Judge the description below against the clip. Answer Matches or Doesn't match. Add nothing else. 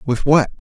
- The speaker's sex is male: Matches